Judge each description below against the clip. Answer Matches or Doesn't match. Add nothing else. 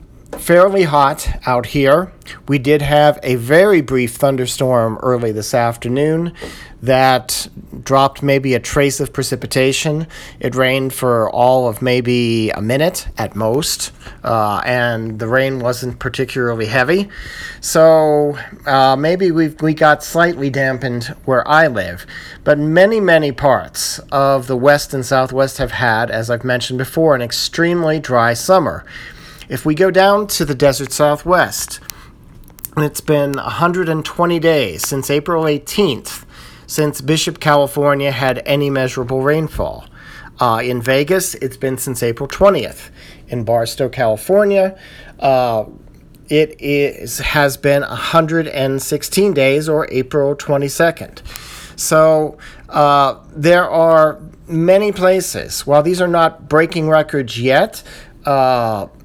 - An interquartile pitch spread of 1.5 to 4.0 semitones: Matches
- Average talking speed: Doesn't match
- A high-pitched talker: Doesn't match